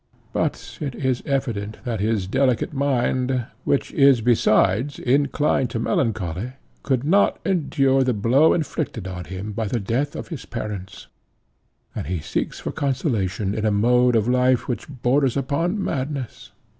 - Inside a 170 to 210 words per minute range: No, average, 150 wpm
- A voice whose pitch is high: No, low, 125 Hz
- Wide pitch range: No, average, 4.3 semitones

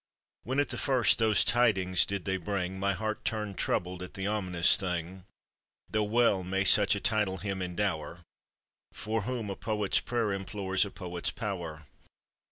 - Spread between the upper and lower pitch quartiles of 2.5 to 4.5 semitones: Yes, average, 2.8 semitones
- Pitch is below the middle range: Yes, low, 100 Hz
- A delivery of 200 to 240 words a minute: No, average, 165 wpm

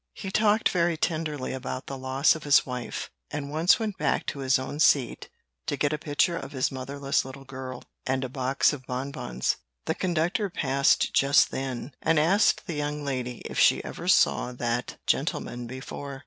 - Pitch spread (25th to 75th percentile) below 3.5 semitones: Yes, average, 3.0 semitones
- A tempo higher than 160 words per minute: Yes, average, 180 wpm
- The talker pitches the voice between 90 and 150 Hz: Yes, medium, 140 Hz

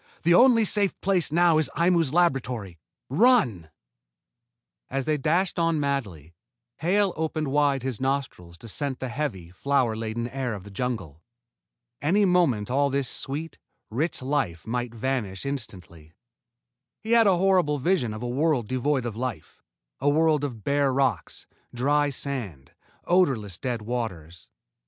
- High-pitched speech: No, low, 135 Hz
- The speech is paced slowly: No, average, 145 wpm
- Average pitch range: No, wide, 5.8 semitones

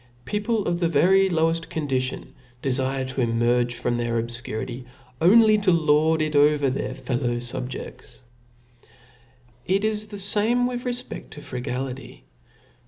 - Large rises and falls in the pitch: Yes, wide, 7.4 semitones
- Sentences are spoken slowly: Yes, slow, 130 wpm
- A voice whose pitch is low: No, medium, 150 Hz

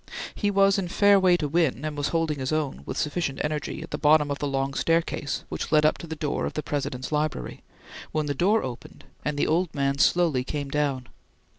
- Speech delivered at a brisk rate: Yes, fast, 225 wpm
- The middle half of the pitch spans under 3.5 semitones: Yes, average, 2.8 semitones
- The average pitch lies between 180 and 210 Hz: No, medium, 150 Hz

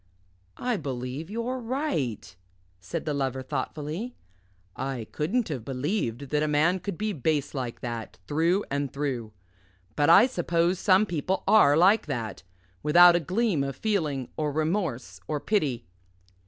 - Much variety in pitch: Yes, wide, 5.9 semitones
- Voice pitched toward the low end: No, medium, 150 Hz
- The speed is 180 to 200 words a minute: No, average, 145 wpm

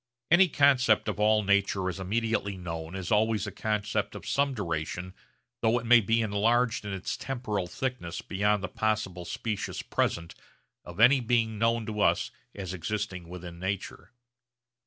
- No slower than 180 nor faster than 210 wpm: No, average, 155 wpm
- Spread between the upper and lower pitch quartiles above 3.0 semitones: Yes, average, 3.6 semitones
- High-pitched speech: No, low, 105 Hz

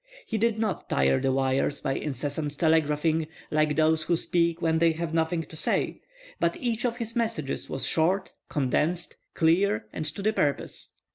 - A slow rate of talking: No, average, 170 wpm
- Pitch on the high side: No, medium, 160 Hz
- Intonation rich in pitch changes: No, average, 3.3 semitones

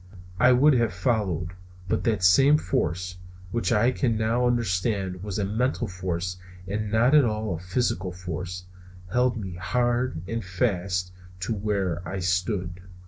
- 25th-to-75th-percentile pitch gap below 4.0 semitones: No, average, 4.6 semitones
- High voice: No, low, 100 Hz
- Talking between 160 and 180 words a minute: No, average, 150 wpm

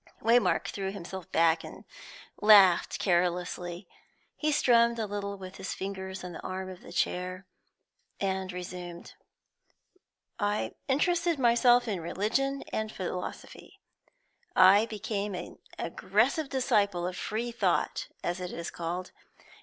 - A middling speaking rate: No, slow, 125 wpm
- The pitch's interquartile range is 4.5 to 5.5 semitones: No, average, 3.9 semitones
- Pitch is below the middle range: No, high, 195 Hz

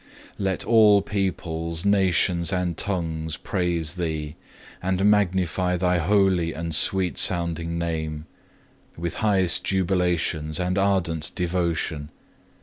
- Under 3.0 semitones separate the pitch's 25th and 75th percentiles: Yes, narrow, 2.5 semitones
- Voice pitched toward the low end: Yes, very low, 90 Hz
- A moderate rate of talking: No, slow, 110 wpm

